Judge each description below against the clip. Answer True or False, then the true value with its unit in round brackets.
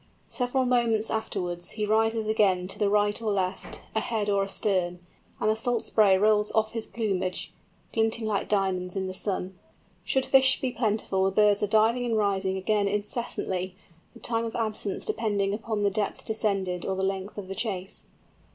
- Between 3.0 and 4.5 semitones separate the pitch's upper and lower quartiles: False (2.5 semitones)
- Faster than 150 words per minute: True (180 wpm)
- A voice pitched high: True (210 Hz)